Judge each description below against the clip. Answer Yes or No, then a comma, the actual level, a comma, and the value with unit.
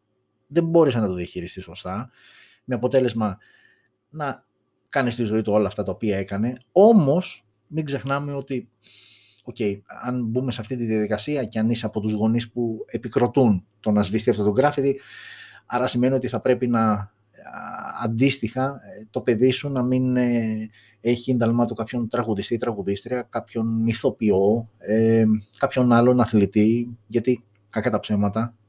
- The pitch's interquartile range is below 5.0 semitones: Yes, average, 2.9 semitones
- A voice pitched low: Yes, low, 115 Hz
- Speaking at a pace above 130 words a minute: Yes, average, 150 wpm